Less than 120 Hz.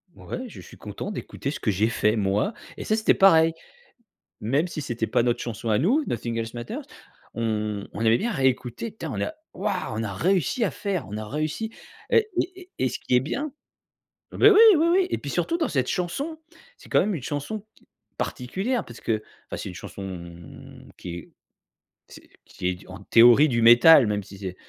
No: low, 125 Hz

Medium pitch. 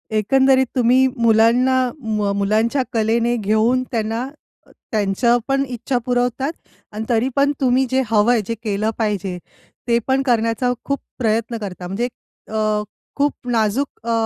No: high, 230 Hz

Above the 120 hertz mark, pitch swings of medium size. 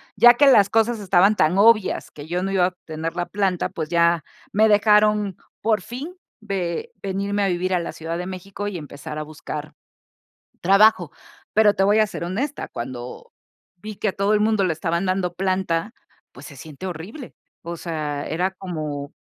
Yes: medium, 185 Hz; average, 3.9 semitones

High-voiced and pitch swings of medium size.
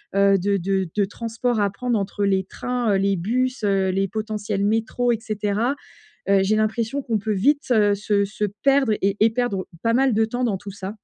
Yes: high, 215 Hz; average, 3.0 semitones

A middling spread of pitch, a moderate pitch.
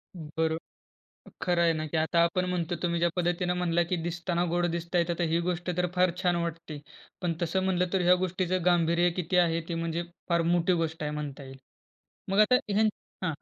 No: narrow, 1.3 semitones; medium, 170 Hz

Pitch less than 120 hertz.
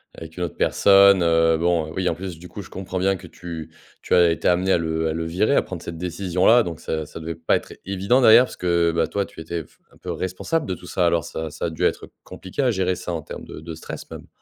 Yes: very low, 85 Hz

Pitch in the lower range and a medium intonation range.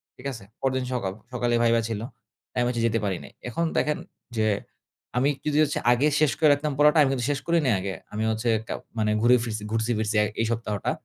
Yes: low, 120 Hz; average, 3.9 semitones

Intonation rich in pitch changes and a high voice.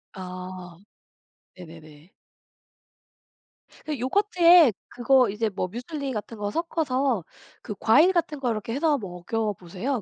Yes: wide, 7.3 semitones; high, 230 Hz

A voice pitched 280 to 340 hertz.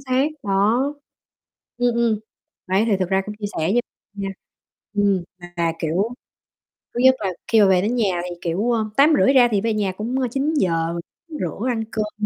No: high, 210 Hz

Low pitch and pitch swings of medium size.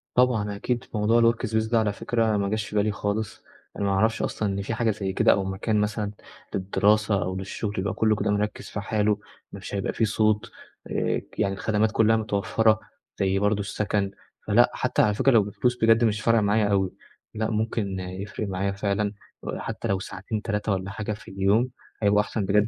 No: low, 105 Hz; narrow, 1.8 semitones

